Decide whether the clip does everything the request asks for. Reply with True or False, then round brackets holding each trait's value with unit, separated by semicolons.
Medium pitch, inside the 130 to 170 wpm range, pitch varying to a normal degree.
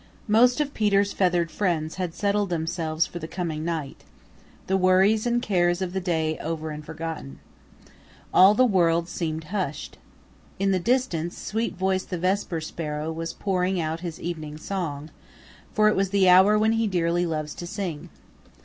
True (175 Hz; 165 wpm; 3.5 semitones)